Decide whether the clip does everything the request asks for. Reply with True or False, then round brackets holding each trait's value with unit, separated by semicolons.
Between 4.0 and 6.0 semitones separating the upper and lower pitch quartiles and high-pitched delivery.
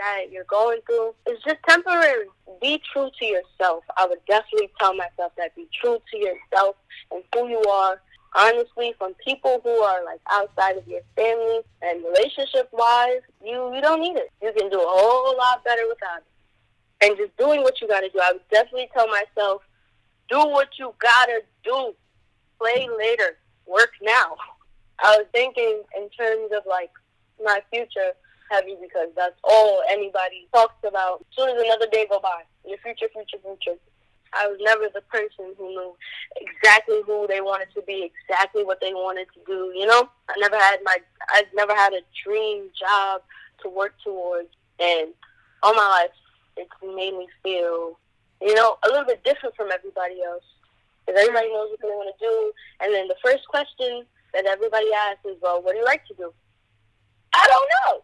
True (4.7 semitones; 210 Hz)